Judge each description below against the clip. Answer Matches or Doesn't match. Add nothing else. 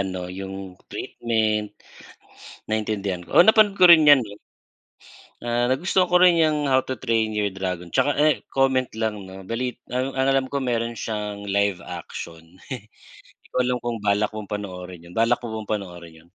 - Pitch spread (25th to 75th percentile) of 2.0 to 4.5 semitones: Doesn't match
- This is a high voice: Doesn't match